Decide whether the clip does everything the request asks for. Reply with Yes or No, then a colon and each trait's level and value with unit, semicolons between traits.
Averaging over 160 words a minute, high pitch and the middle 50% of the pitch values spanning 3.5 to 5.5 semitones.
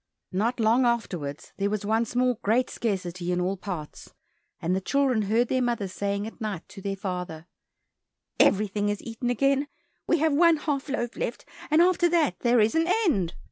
Yes: average, 180 wpm; high, 220 Hz; average, 4.8 semitones